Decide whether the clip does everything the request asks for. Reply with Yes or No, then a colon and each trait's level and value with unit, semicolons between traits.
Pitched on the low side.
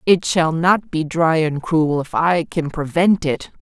No: medium, 165 Hz